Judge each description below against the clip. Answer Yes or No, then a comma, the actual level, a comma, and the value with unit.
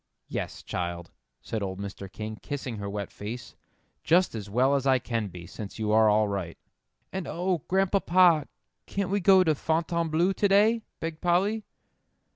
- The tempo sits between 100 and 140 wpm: No, average, 165 wpm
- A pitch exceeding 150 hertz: No, medium, 140 Hz